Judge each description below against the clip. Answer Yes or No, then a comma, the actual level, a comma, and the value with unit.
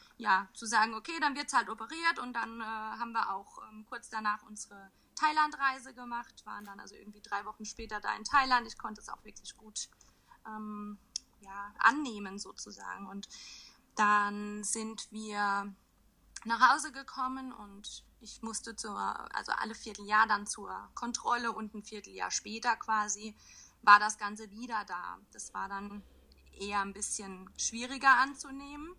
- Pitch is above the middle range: Yes, high, 220 Hz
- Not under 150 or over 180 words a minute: Yes, average, 155 wpm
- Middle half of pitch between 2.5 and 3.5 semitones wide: Yes, average, 2.8 semitones